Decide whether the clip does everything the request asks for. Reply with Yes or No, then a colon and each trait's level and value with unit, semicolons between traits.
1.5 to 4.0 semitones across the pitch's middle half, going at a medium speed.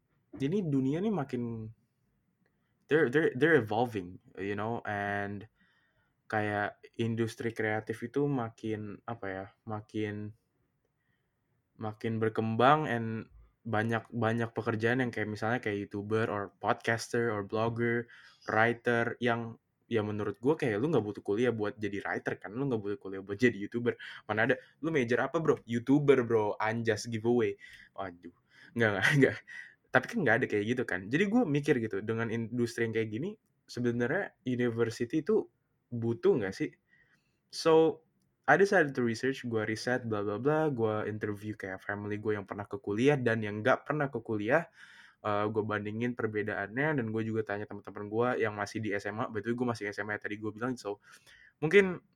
No: average, 2.8 semitones; fast, 160 wpm